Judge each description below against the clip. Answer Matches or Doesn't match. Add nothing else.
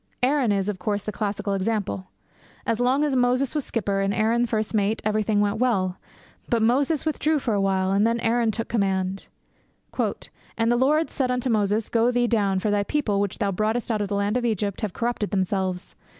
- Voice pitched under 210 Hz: Doesn't match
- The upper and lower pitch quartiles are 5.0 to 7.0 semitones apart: Doesn't match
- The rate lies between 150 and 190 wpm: Doesn't match